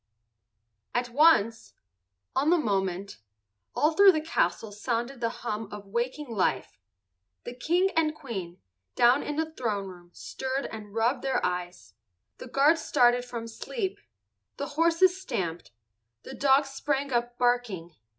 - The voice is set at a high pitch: Yes, high, 240 Hz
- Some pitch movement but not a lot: No, wide, 6.6 semitones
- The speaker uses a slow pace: Yes, slow, 130 wpm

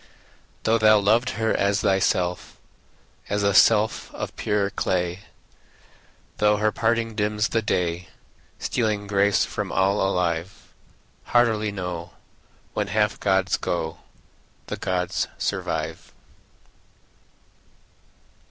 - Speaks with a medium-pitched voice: No, low, 100 Hz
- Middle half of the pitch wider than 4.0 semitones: No, average, 2.7 semitones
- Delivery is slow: Yes, slow, 105 wpm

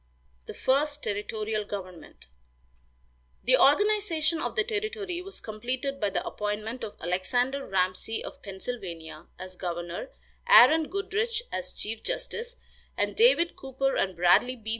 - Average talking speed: No, slow, 130 wpm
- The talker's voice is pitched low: No, very high, 250 Hz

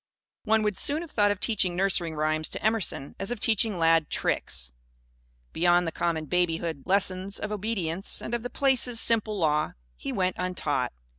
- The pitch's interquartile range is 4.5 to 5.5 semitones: Yes, average, 4.8 semitones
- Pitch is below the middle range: No, medium, 185 Hz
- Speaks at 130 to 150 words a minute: No, average, 175 wpm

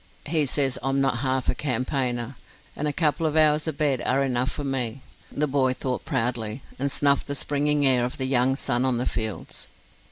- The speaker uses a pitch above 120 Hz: Yes, low, 135 Hz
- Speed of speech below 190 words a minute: No, average, 200 wpm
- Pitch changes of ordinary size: No, narrow, 2.3 semitones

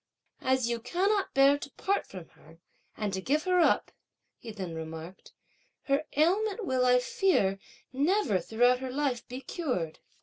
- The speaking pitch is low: No, very high, 255 Hz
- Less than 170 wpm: Yes, average, 160 wpm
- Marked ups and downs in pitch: Yes, wide, 8.0 semitones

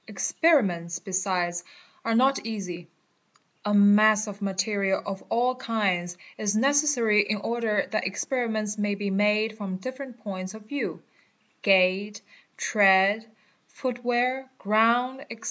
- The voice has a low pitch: No, high, 210 Hz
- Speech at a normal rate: No, slow, 120 wpm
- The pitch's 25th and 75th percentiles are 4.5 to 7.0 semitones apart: No, average, 3.4 semitones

